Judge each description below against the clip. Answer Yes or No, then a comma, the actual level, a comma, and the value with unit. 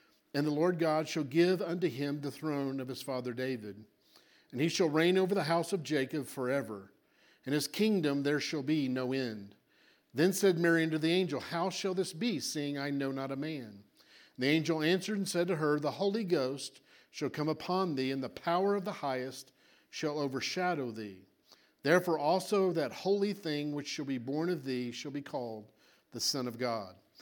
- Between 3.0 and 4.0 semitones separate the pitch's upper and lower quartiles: No, average, 4.7 semitones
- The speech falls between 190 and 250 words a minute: Yes, average, 200 wpm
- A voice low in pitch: No, medium, 150 Hz